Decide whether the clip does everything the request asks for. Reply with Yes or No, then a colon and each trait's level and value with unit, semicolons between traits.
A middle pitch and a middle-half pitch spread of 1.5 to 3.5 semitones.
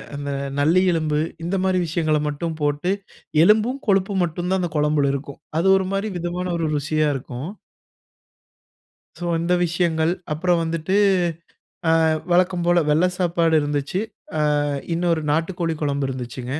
Yes: medium, 165 Hz; average, 3.2 semitones